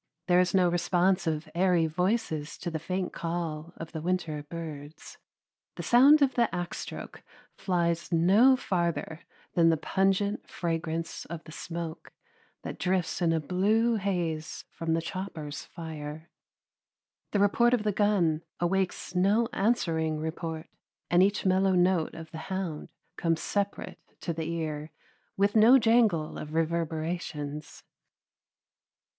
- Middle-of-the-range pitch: Yes, medium, 170 Hz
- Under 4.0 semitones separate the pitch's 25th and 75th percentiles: Yes, average, 3.2 semitones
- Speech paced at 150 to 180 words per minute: No, average, 140 wpm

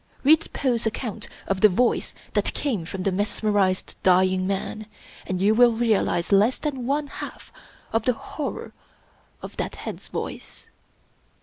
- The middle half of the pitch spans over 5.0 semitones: No, average, 4.5 semitones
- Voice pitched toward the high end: Yes, high, 215 Hz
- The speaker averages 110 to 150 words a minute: Yes, average, 145 wpm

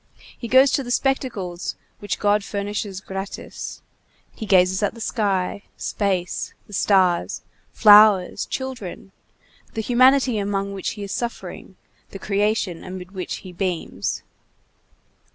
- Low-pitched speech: No, high, 200 Hz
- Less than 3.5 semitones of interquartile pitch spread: Yes, average, 2.8 semitones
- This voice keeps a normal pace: No, slow, 125 wpm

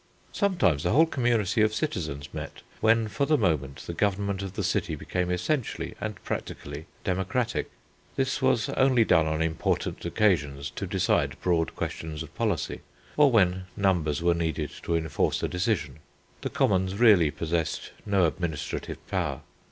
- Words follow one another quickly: No, average, 150 wpm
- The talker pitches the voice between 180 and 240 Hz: No, very low, 90 Hz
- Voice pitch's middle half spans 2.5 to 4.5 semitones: No, average, 5.2 semitones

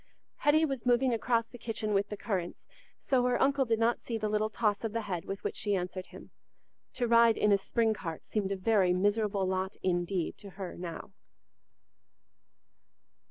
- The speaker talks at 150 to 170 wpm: No, average, 185 wpm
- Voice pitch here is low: No, high, 210 Hz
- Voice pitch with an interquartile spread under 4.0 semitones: Yes, average, 3.4 semitones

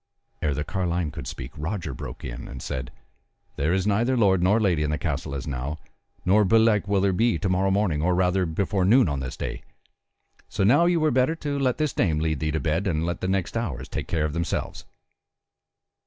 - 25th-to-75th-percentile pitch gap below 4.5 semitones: No, wide, 5.4 semitones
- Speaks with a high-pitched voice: No, very low, 90 Hz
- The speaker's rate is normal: No, fast, 215 wpm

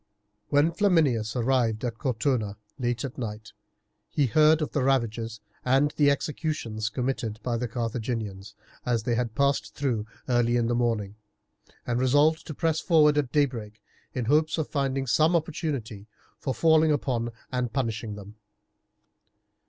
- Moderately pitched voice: No, low, 125 Hz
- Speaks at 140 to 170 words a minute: Yes, average, 145 wpm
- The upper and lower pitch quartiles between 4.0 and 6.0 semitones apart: Yes, average, 4.4 semitones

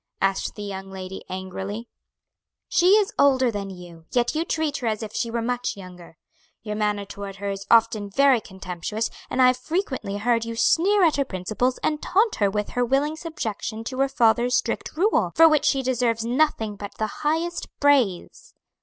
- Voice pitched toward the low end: No, high, 230 Hz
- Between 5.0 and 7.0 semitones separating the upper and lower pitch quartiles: Yes, wide, 5.6 semitones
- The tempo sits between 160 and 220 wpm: Yes, average, 190 wpm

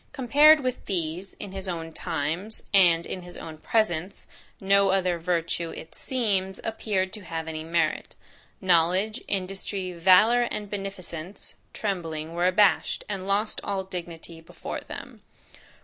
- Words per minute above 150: No, slow, 135 wpm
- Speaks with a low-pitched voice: No, medium, 185 Hz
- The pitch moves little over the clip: No, average, 3.2 semitones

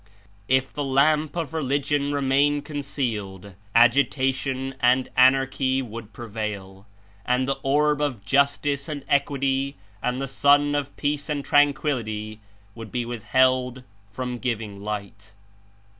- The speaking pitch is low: Yes, low, 130 Hz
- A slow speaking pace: Yes, slow, 125 wpm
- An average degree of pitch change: Yes, average, 3.3 semitones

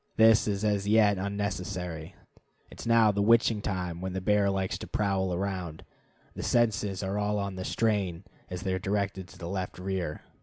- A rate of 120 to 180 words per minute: No, average, 190 wpm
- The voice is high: No, low, 100 Hz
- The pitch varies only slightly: Yes, narrow, 2.0 semitones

